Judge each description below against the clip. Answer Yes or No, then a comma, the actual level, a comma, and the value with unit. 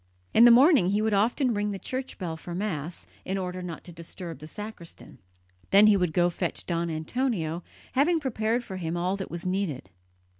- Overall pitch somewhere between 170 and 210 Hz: Yes, high, 190 Hz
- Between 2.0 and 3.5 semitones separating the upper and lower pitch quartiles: No, average, 4.5 semitones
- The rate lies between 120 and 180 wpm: No, average, 200 wpm